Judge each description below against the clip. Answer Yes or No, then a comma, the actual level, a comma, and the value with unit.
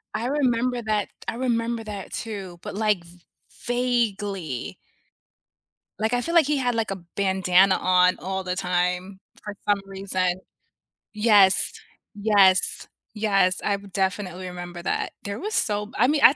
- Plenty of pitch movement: No, average, 3.6 semitones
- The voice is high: Yes, high, 200 Hz